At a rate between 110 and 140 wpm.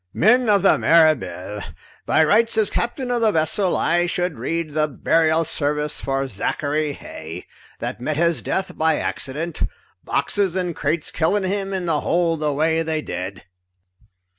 No: average, 160 wpm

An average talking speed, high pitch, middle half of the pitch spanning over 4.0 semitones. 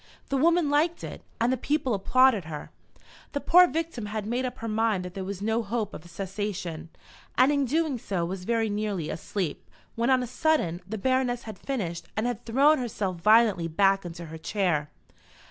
Yes: average, 190 wpm; high, 220 Hz; wide, 5.6 semitones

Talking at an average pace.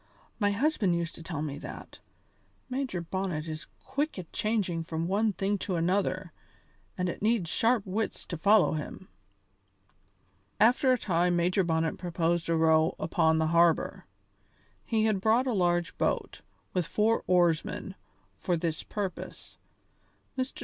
Yes: average, 145 wpm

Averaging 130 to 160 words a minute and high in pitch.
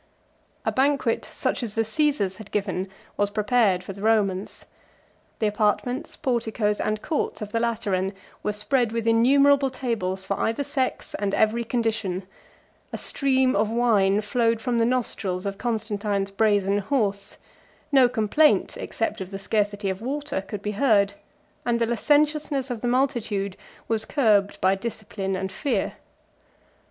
Yes: average, 150 wpm; high, 220 Hz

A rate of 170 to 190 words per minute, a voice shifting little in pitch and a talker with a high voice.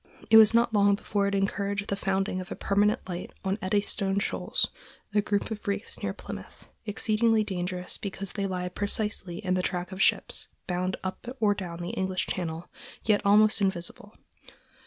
Yes: average, 175 wpm; narrow, 2.0 semitones; high, 200 Hz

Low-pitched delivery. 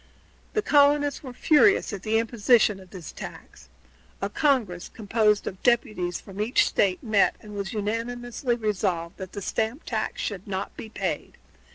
No: high, 215 Hz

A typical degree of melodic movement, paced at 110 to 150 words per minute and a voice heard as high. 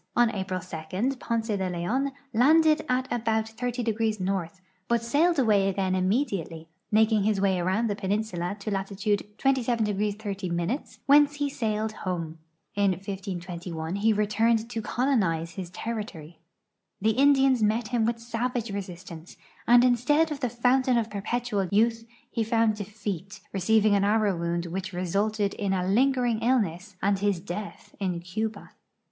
Yes: average, 3.8 semitones; average, 145 wpm; high, 210 Hz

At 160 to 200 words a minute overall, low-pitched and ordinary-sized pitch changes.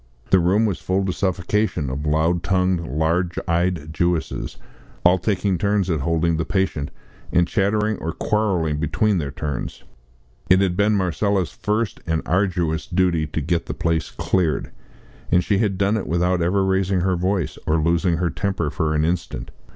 Yes: average, 170 wpm; very low, 90 Hz; average, 3.0 semitones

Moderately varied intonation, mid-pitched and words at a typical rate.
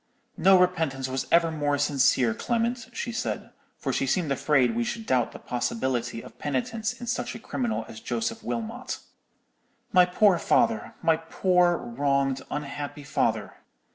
No: wide, 8.6 semitones; medium, 160 Hz; average, 145 wpm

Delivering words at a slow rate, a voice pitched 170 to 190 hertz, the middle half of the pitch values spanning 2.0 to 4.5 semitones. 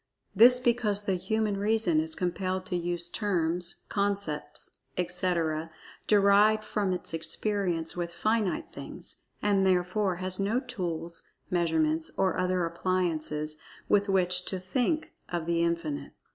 Yes: slow, 130 wpm; medium, 185 Hz; average, 3.2 semitones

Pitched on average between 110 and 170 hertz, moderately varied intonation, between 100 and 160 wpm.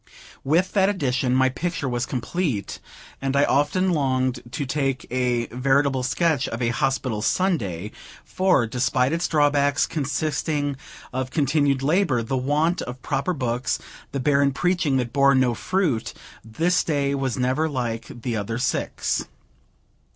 Yes: low, 135 Hz; average, 3.3 semitones; average, 145 wpm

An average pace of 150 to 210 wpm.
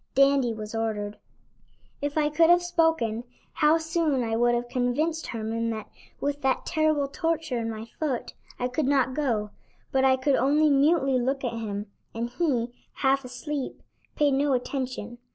Yes: average, 165 wpm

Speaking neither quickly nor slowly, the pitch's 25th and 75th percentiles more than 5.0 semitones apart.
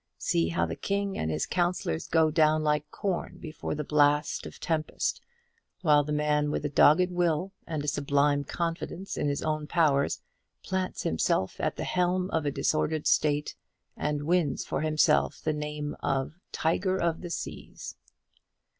No: average, 165 wpm; narrow, 2.6 semitones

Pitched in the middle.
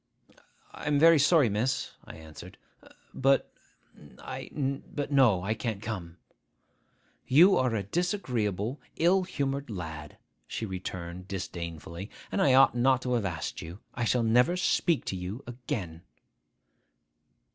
No: low, 120 Hz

